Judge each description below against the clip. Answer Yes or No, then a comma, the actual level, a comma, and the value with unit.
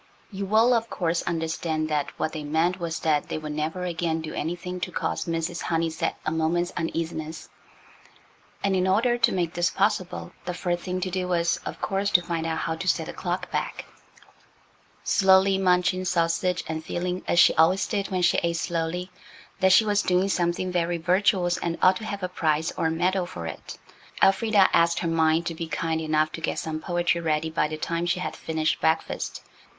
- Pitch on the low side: No, medium, 175 Hz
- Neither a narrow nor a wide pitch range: No, narrow, 2.2 semitones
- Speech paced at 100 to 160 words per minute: No, average, 200 wpm